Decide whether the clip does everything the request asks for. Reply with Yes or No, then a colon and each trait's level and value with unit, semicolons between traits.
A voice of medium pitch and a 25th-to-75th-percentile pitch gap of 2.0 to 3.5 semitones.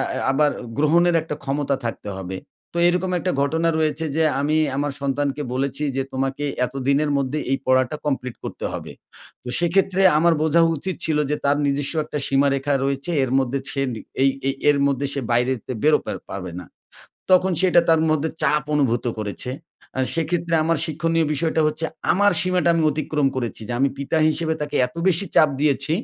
Yes: medium, 145 Hz; average, 3.0 semitones